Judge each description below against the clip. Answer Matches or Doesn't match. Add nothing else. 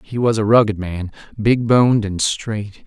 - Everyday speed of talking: Matches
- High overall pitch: Doesn't match